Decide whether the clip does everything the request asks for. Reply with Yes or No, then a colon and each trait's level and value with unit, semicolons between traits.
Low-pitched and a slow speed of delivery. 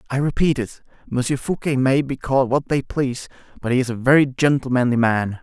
No: low, 130 Hz; average, 200 wpm